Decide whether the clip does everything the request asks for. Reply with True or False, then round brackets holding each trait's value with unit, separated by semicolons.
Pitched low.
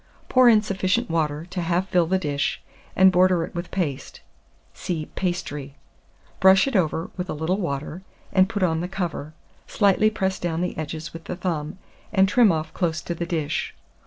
False (175 Hz)